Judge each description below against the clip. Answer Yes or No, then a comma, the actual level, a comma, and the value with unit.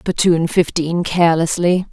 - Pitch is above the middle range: No, medium, 170 Hz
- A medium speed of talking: No, slow, 95 wpm